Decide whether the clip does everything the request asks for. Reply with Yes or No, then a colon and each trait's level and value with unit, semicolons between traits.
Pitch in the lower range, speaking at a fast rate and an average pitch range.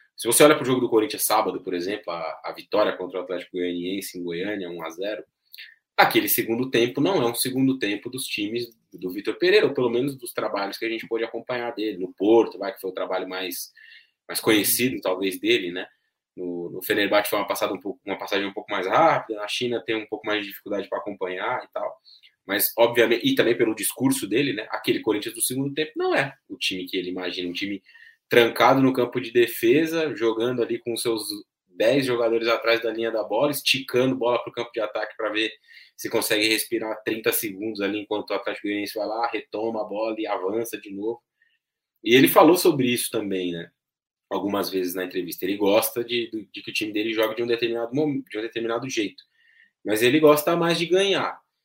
No: low, 115 Hz; fast, 215 wpm; wide, 7.9 semitones